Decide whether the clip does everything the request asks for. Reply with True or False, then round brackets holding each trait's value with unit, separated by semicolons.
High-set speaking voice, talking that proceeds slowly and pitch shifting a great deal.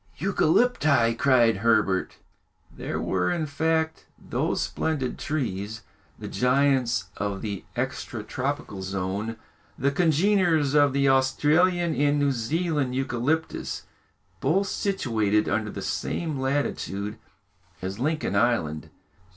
False (135 Hz; 110 wpm; 6.4 semitones)